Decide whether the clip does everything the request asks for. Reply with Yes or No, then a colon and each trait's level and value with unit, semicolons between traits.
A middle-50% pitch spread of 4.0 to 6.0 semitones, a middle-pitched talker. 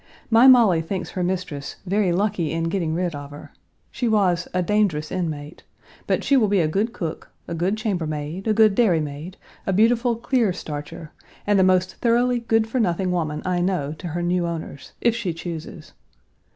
Yes: average, 4.6 semitones; medium, 180 Hz